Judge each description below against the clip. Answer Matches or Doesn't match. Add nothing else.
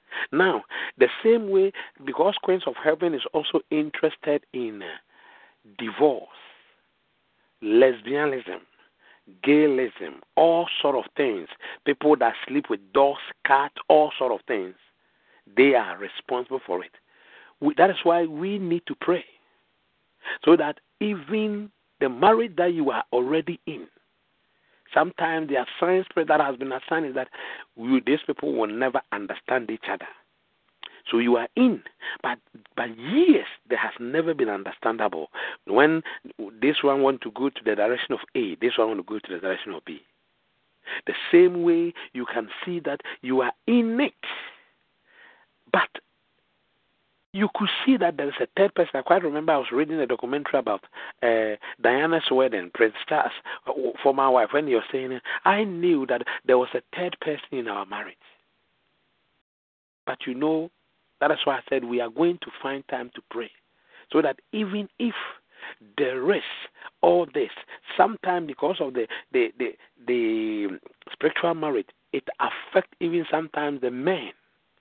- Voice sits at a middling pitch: Matches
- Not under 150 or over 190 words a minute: Matches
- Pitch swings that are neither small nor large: Doesn't match